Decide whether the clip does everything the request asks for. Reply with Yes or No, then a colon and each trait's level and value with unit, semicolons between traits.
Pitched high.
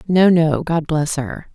No: medium, 160 Hz